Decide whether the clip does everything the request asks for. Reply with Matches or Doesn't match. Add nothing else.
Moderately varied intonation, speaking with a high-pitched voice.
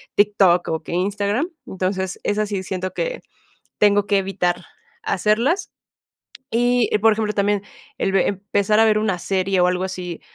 Doesn't match